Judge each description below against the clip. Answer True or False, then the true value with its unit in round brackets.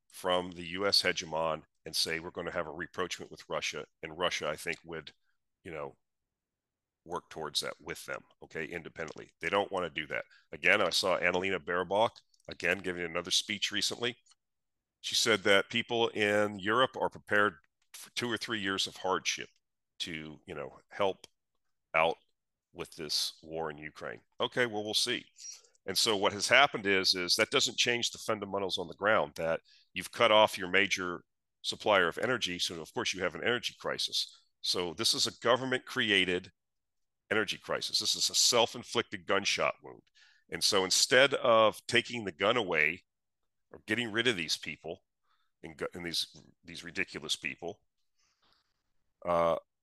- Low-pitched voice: True (95 Hz)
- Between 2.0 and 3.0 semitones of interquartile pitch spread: False (3.8 semitones)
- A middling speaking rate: True (170 wpm)